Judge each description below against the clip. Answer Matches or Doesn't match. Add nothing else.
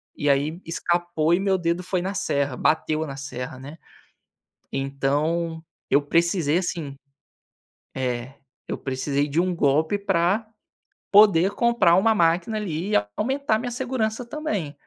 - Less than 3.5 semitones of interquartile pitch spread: Doesn't match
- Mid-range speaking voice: Matches